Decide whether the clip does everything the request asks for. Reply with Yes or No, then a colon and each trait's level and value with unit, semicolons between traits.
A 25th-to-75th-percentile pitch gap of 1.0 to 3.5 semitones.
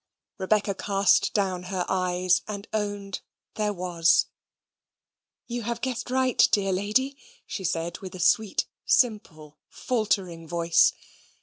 Yes: average, 3.2 semitones